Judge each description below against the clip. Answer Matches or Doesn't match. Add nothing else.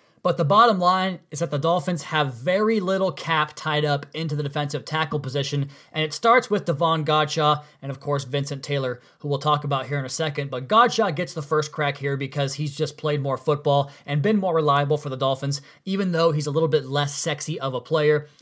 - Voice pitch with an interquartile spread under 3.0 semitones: Matches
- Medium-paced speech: Doesn't match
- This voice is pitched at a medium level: Matches